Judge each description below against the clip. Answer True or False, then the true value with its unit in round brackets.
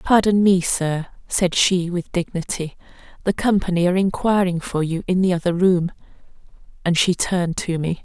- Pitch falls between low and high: True (180 Hz)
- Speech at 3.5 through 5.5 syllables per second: True (5.0 syllables/s)